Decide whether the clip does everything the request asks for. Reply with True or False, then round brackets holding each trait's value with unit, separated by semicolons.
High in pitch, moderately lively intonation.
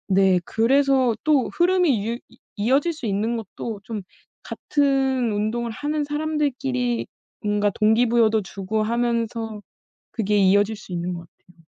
True (230 Hz; 4.4 semitones)